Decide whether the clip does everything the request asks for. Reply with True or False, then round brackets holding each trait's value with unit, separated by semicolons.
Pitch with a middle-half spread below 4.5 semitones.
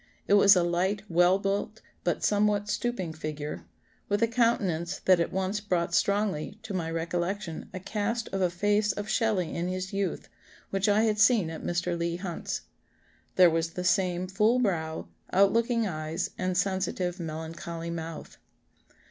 True (3.3 semitones)